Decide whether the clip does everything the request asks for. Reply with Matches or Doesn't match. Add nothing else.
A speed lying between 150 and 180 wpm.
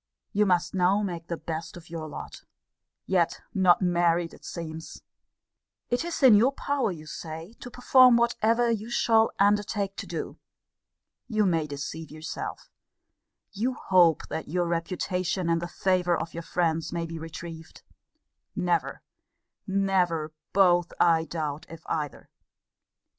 Doesn't match